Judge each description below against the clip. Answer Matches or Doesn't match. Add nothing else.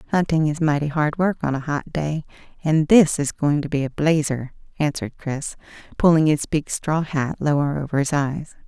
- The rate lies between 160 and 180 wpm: Doesn't match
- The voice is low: Doesn't match